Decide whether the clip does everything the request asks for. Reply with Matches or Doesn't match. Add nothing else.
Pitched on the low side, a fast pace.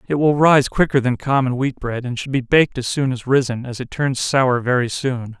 Matches